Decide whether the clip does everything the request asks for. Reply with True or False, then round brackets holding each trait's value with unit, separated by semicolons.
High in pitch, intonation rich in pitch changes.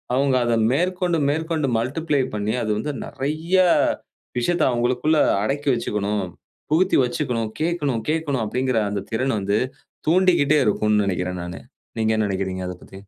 False (130 Hz; 6.6 semitones)